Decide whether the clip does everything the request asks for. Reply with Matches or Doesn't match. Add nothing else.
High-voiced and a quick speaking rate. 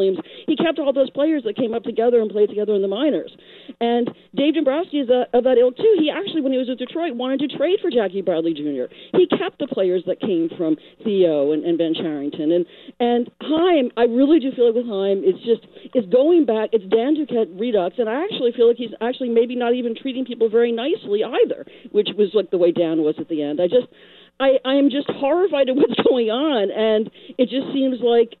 Matches